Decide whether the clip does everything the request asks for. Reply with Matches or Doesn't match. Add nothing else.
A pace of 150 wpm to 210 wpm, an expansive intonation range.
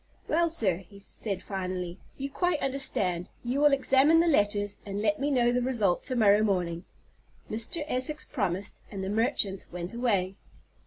Matches